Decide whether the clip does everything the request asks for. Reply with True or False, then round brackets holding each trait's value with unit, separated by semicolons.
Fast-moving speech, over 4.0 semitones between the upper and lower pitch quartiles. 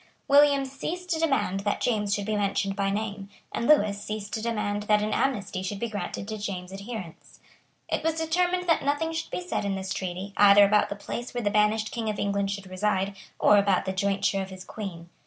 False (215 wpm; 3.4 semitones)